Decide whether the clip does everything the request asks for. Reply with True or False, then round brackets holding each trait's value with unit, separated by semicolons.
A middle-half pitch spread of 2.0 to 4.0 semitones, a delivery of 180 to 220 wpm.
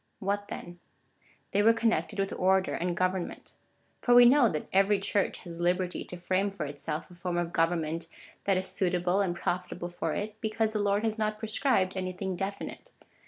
True (2.8 semitones; 185 wpm)